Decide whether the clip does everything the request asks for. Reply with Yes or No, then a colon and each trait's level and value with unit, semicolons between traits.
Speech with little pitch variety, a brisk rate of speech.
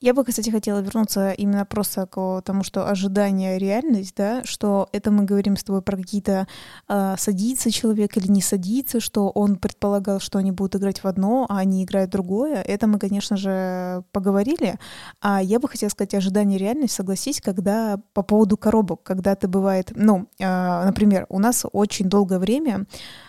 Yes: narrow, 1.6 semitones; fast, 180 wpm